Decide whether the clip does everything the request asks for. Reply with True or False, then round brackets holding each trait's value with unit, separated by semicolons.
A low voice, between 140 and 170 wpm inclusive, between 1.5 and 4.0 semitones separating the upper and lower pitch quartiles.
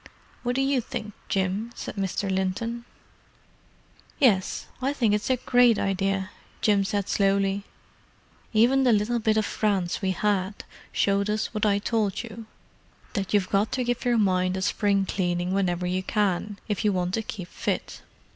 False (205 Hz; 165 wpm; 2.8 semitones)